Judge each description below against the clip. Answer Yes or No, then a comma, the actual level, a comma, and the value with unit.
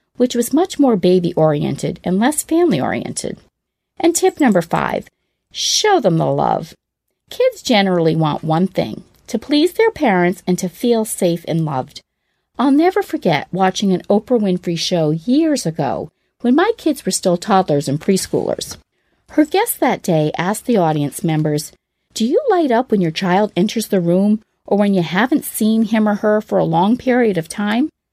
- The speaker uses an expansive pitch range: Yes, wide, 6.9 semitones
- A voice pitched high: Yes, high, 205 Hz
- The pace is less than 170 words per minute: No, average, 175 wpm